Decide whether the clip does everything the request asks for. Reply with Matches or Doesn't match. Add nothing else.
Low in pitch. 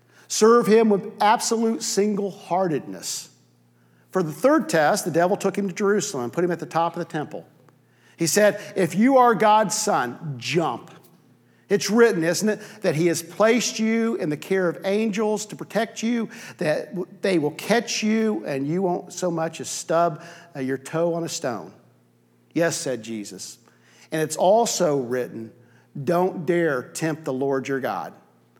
Doesn't match